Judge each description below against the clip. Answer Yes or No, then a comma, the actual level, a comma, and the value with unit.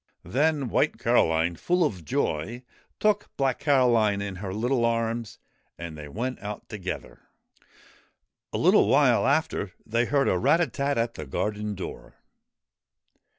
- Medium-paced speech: Yes, average, 145 wpm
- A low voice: Yes, low, 115 Hz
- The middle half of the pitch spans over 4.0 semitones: Yes, wide, 5.4 semitones